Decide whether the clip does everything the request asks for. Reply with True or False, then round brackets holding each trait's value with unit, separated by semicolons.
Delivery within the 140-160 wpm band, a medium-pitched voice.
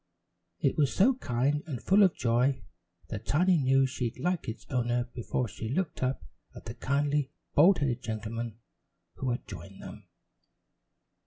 False (155 wpm; 130 Hz)